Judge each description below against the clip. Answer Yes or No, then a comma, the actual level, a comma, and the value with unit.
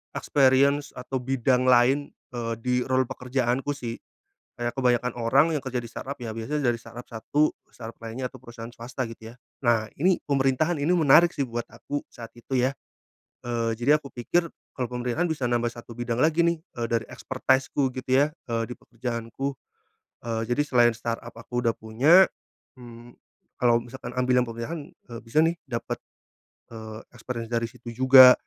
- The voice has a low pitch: Yes, low, 125 Hz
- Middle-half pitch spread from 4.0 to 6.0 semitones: No, narrow, 2.5 semitones